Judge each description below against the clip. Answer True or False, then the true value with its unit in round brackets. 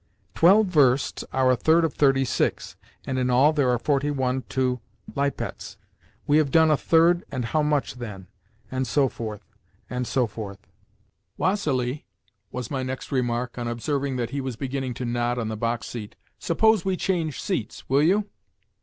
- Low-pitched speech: True (130 Hz)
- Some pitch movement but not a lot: True (3.5 semitones)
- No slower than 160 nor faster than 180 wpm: True (175 wpm)